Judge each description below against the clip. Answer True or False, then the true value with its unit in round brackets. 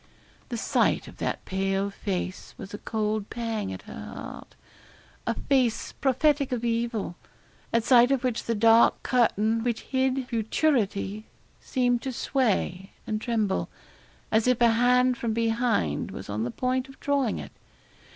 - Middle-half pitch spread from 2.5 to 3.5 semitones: True (3.0 semitones)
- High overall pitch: True (230 Hz)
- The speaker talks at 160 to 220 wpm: False (150 wpm)